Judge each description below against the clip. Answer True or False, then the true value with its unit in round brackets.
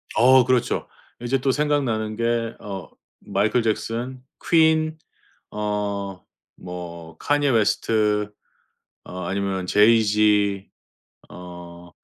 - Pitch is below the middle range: True (105 Hz)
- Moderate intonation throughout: True (3.9 semitones)